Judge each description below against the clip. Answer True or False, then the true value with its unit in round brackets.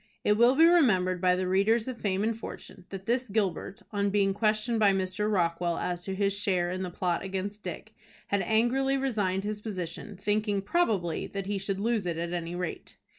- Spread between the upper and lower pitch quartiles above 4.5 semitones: False (2.9 semitones)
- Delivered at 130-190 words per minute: False (200 wpm)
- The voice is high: True (200 Hz)